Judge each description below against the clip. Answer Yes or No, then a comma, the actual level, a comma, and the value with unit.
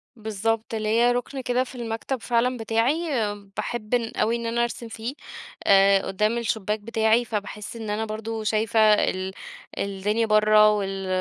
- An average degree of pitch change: No, narrow, 1.7 semitones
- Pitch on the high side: Yes, high, 220 Hz